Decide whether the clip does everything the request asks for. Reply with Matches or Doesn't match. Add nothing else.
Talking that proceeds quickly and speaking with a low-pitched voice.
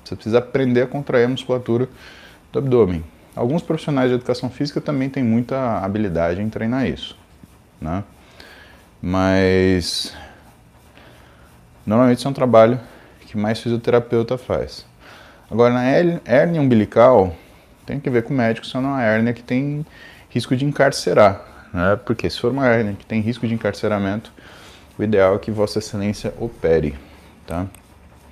Doesn't match